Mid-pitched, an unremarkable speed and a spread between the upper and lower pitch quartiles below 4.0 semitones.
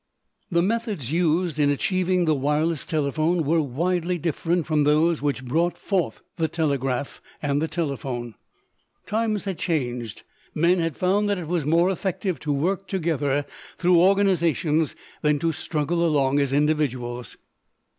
Yes: medium, 160 Hz; average, 145 wpm; average, 3.6 semitones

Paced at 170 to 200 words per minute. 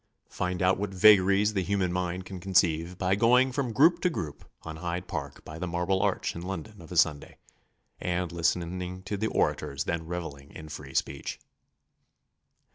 Yes: average, 175 wpm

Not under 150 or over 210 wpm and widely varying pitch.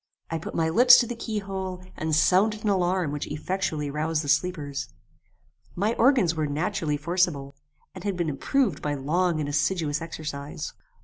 No: average, 170 wpm; average, 4.3 semitones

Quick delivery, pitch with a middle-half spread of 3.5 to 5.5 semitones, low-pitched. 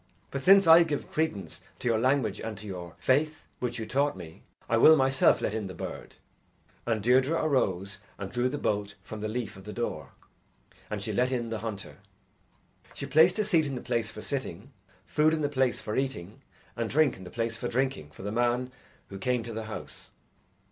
Yes: fast, 210 wpm; average, 4.5 semitones; low, 120 Hz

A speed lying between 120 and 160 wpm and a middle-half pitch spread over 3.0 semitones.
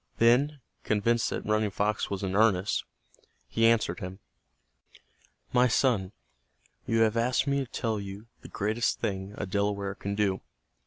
No: average, 150 wpm; average, 2.7 semitones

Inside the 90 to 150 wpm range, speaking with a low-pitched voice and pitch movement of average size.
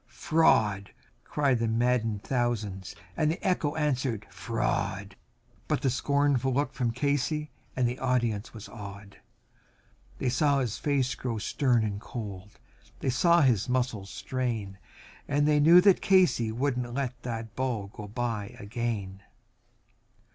Yes: average, 140 wpm; low, 120 Hz; average, 4.5 semitones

